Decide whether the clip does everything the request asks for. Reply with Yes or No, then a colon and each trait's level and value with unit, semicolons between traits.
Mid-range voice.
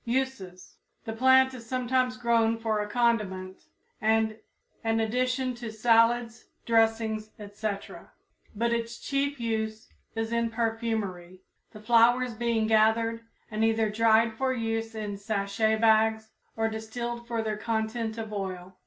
No: high, 225 Hz